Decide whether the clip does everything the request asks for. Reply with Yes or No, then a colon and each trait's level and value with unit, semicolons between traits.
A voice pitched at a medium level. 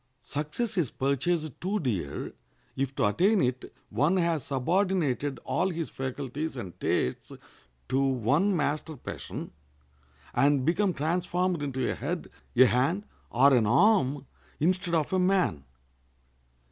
Yes: medium, 145 Hz